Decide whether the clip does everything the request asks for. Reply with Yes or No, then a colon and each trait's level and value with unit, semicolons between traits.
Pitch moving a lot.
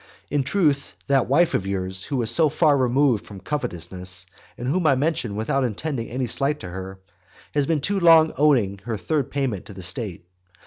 Yes: wide, 7.0 semitones